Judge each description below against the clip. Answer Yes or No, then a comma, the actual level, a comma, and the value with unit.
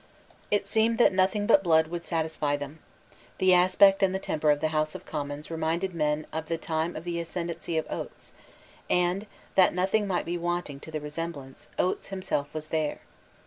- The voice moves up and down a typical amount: Yes, average, 3.2 semitones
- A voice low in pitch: No, medium, 170 Hz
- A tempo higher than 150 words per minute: Yes, average, 185 wpm